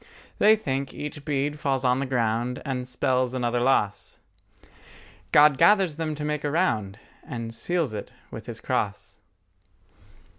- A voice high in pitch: No, low, 135 Hz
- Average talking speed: Yes, average, 145 wpm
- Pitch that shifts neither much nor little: Yes, average, 3.3 semitones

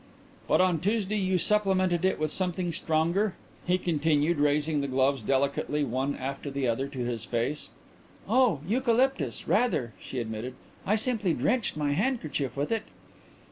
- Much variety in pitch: Yes, wide, 6.2 semitones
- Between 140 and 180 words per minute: Yes, average, 150 wpm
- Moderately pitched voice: Yes, medium, 155 Hz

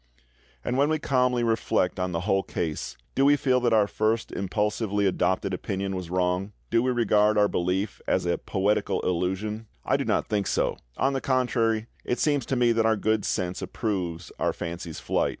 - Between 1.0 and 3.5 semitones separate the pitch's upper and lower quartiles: No, average, 4.3 semitones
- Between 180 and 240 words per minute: Yes, average, 190 wpm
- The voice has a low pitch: Yes, low, 105 Hz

